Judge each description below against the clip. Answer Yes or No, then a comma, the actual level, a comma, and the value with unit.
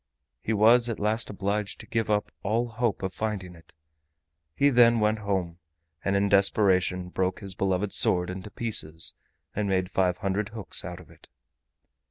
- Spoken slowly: No, average, 170 wpm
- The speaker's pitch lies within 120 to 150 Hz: No, low, 100 Hz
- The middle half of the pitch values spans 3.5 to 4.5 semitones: No, average, 2.8 semitones